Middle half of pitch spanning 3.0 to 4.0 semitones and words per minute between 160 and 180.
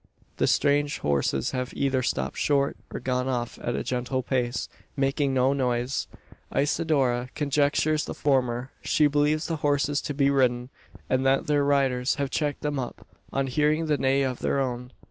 No: narrow, 2.4 semitones; average, 170 wpm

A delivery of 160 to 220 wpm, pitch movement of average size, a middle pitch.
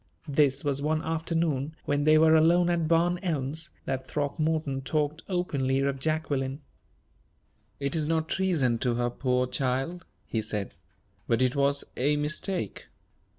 No: average, 145 wpm; average, 3.3 semitones; medium, 145 Hz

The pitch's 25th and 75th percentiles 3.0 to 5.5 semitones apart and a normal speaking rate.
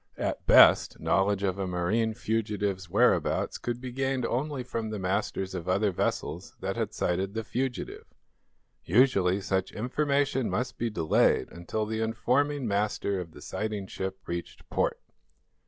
Yes: average, 4.4 semitones; average, 150 wpm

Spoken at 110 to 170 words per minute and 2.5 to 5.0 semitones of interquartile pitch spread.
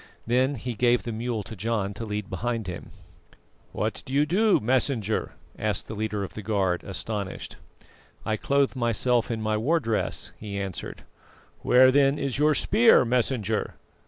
Yes: average, 160 wpm; average, 3.7 semitones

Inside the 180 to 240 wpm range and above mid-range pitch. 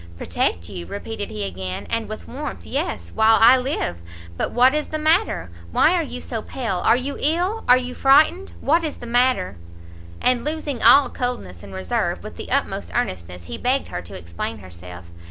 Yes: average, 190 wpm; high, 240 Hz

